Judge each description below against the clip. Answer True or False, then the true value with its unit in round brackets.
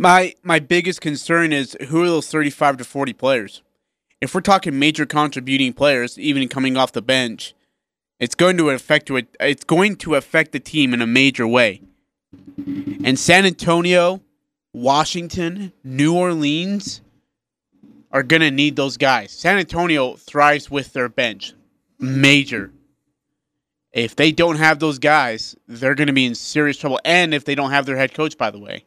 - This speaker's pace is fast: False (165 wpm)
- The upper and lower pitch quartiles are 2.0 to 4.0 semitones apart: True (3.7 semitones)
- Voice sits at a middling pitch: True (150 Hz)